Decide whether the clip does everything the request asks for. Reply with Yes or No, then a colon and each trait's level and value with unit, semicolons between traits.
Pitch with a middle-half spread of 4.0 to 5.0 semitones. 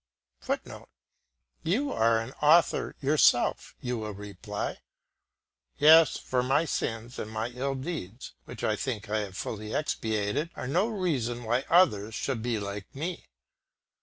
No: wide, 5.6 semitones